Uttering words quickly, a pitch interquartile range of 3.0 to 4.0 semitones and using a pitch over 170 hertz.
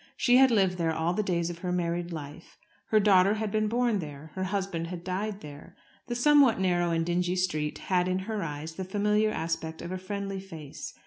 Yes: fast, 210 wpm; average, 3.7 semitones; medium, 185 Hz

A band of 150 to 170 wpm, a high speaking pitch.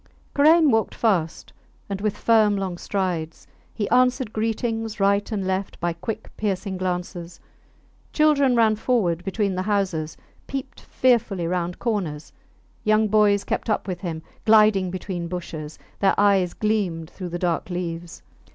No: average, 140 wpm; high, 195 Hz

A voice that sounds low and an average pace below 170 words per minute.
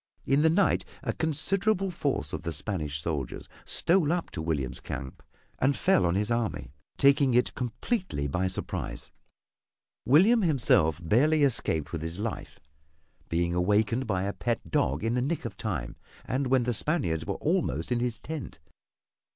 Yes: low, 115 Hz; average, 160 wpm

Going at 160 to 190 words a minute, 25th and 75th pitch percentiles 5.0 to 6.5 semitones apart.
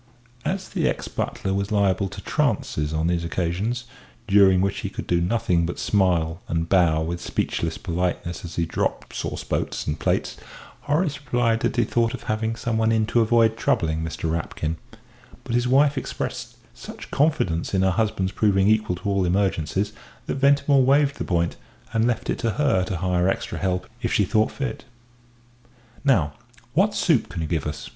Yes: average, 180 wpm; average, 5.3 semitones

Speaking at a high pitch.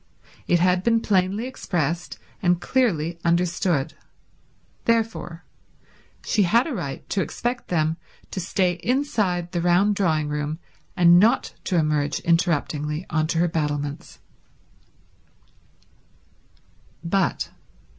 No: medium, 175 Hz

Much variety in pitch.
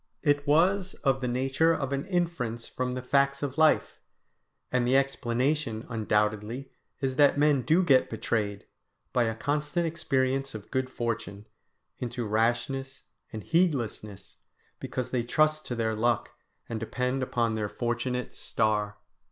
No: average, 3.7 semitones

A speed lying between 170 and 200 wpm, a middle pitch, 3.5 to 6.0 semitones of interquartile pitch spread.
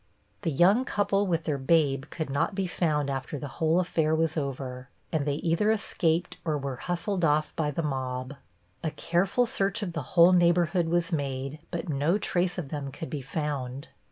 Yes: average, 185 wpm; medium, 160 Hz; average, 3.9 semitones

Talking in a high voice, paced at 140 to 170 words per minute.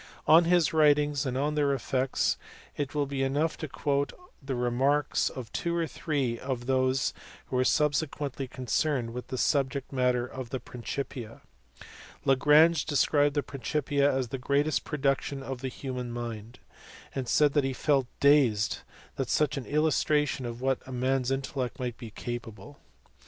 No: low, 135 Hz; average, 155 wpm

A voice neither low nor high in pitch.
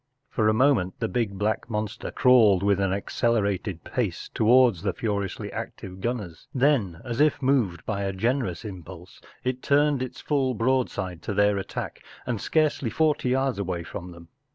No: low, 110 Hz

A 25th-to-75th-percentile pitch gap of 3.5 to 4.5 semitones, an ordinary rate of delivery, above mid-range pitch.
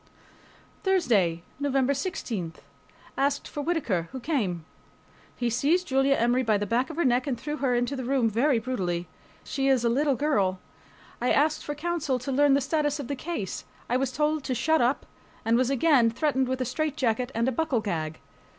Yes: average, 3.9 semitones; average, 190 wpm; very high, 260 Hz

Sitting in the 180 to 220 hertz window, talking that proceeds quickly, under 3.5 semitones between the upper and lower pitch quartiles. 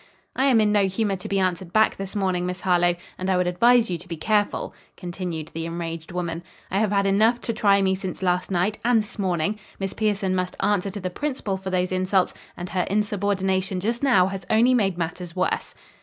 Yes: high, 190 Hz; fast, 215 wpm; narrow, 2.5 semitones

